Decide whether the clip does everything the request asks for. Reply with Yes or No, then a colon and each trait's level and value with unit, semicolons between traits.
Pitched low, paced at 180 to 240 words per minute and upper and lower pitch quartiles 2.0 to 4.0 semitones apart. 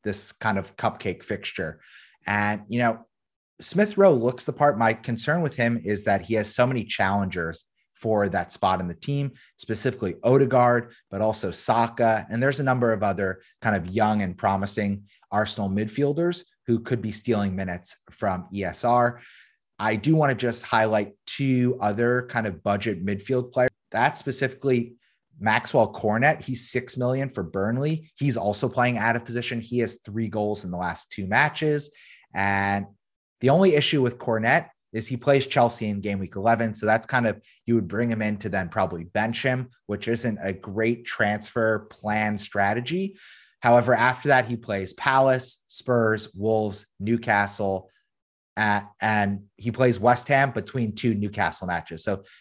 No: low, 115 Hz; average, 170 wpm; average, 3.5 semitones